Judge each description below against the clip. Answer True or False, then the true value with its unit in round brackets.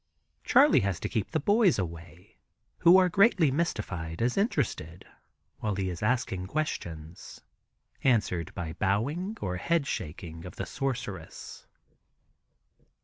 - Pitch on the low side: True (105 Hz)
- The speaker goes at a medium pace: False (125 wpm)